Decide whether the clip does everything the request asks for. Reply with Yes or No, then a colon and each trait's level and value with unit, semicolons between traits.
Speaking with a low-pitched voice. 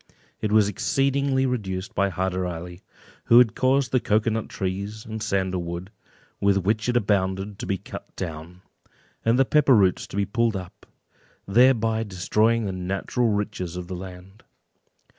Yes: low, 100 Hz